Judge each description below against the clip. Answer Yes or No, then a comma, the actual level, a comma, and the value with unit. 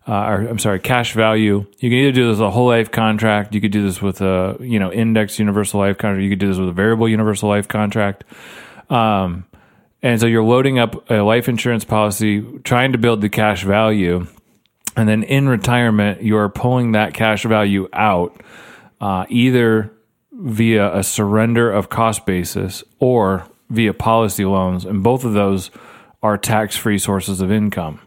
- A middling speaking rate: Yes, average, 180 wpm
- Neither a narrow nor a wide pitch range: No, narrow, 2.3 semitones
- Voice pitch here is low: Yes, low, 105 Hz